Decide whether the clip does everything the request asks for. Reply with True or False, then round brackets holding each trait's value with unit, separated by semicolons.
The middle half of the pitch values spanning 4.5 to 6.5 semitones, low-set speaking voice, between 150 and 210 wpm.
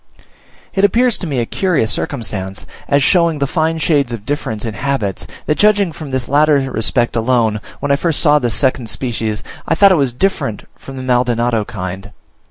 True (5.4 semitones; 130 Hz; 185 wpm)